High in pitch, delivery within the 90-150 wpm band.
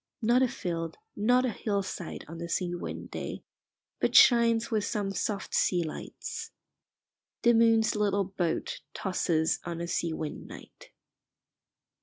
Yes: high, 195 Hz; average, 140 wpm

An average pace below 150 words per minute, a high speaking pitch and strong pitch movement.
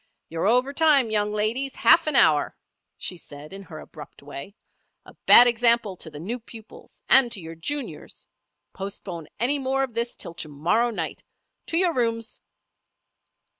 No: average, 165 wpm; high, 225 Hz; wide, 6.8 semitones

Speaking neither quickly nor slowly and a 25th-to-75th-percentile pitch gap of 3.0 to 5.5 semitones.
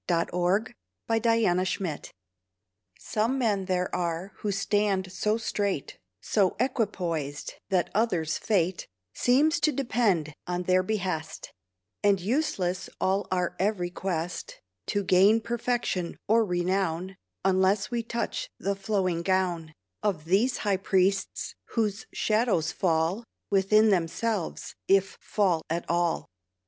No: slow, 120 wpm; average, 3.5 semitones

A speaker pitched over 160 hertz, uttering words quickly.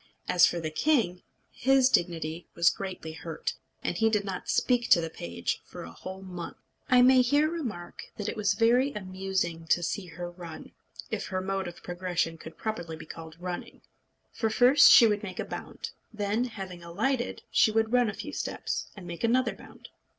No: high, 190 Hz; average, 190 wpm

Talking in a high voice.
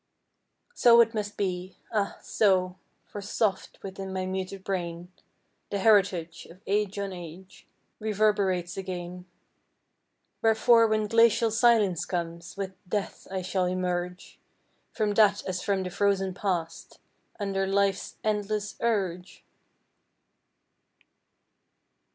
Yes: high, 195 Hz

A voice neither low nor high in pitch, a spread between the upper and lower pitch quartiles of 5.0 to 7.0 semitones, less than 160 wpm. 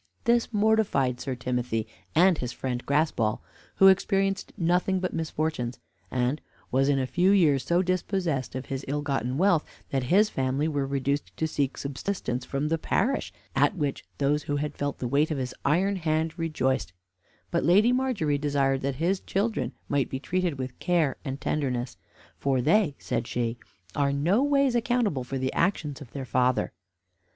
No: medium, 145 Hz; wide, 5.5 semitones; average, 170 wpm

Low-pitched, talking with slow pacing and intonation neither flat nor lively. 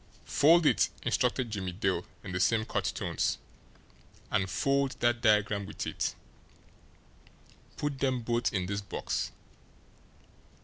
Yes: low, 115 Hz; slow, 125 wpm; average, 5.0 semitones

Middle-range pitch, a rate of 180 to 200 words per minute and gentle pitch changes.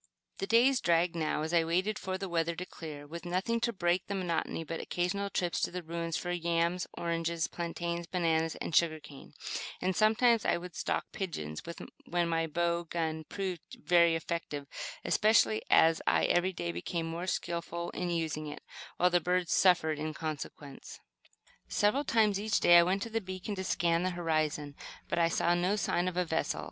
Yes: medium, 170 Hz; average, 185 wpm; narrow, 2.1 semitones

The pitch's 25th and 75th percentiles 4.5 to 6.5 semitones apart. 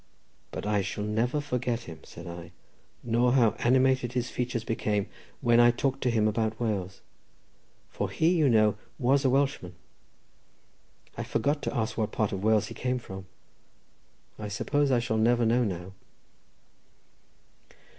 No: average, 3.1 semitones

